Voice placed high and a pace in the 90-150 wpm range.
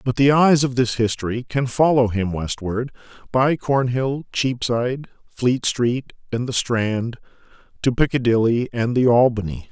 No: low, 120 Hz; average, 140 wpm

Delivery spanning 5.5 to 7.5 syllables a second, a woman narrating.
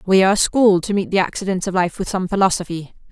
Yes: 6.7 syllables/s; female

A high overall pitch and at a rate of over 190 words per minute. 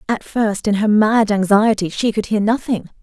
Yes: high, 215 Hz; average, 200 wpm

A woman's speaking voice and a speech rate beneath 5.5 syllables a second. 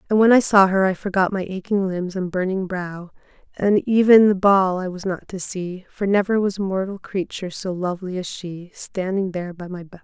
Yes: female; 5.2 syllables/s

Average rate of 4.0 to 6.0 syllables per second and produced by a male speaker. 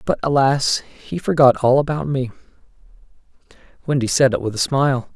Yes: 5.3 syllables/s; male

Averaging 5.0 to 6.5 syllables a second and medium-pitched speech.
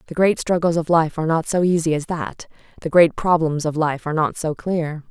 Yes: 5.5 syllables/s; medium, 160 Hz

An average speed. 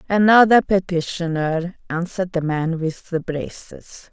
No: slow, 115 wpm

